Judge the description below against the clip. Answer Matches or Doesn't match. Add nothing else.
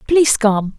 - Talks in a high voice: Matches